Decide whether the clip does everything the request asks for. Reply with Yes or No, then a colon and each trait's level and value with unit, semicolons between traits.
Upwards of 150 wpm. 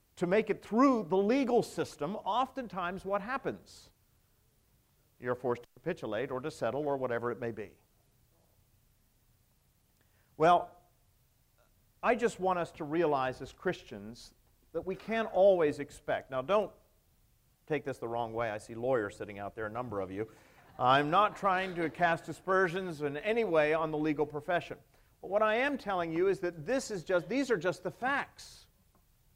Yes: average, 170 wpm